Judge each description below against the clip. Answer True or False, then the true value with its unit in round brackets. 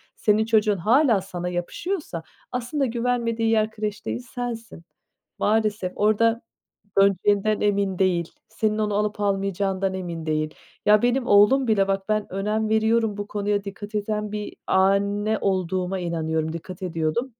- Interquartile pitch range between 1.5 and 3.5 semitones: True (2.6 semitones)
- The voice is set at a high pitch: True (205 Hz)